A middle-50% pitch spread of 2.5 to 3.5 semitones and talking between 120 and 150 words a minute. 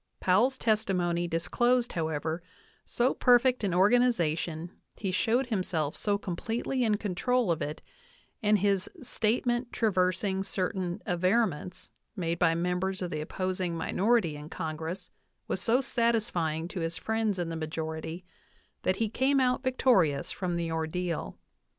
No: average, 5.2 semitones; average, 140 wpm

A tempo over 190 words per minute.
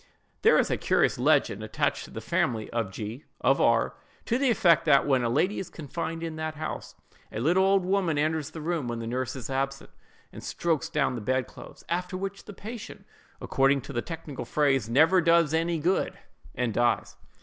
Yes: average, 200 wpm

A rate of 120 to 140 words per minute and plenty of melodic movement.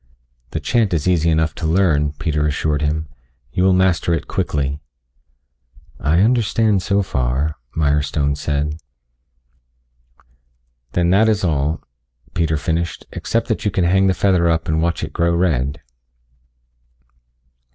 No: slow, 135 wpm; average, 3.6 semitones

